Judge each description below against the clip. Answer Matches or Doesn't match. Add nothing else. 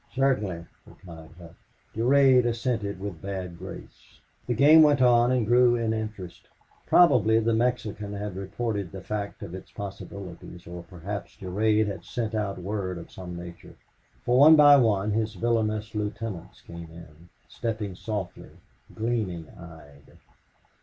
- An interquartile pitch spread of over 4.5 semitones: Doesn't match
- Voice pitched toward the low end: Matches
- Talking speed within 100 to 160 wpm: Matches